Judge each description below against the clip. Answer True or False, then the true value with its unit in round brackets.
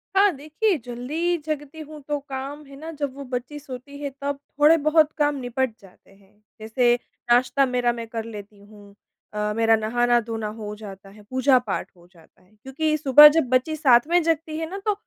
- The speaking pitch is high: True (260 Hz)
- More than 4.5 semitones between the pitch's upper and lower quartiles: True (5.1 semitones)